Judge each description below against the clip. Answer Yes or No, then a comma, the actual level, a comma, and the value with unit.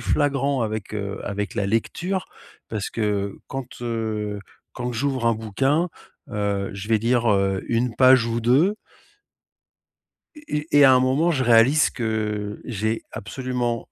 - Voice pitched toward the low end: Yes, low, 115 Hz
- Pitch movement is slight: No, average, 3.9 semitones